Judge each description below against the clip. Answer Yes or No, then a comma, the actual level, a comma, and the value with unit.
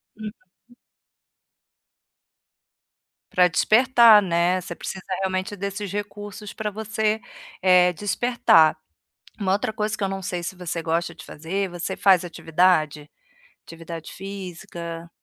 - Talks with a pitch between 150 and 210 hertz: Yes, medium, 185 Hz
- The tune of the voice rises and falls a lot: No, average, 3.4 semitones